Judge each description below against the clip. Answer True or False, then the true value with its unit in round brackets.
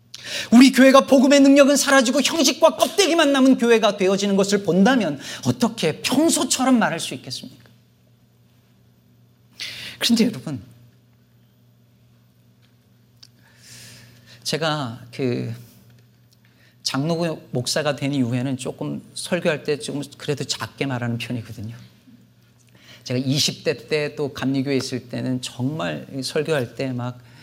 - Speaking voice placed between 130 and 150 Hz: True (135 Hz)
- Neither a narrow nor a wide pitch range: False (9.0 semitones)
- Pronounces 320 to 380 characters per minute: False (245 characters per minute)